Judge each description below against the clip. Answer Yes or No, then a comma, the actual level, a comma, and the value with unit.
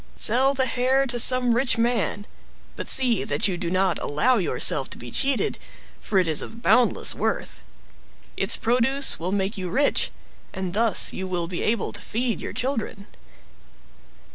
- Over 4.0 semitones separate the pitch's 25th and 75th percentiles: Yes, average, 5.3 semitones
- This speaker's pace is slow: No, average, 165 wpm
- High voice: Yes, high, 225 Hz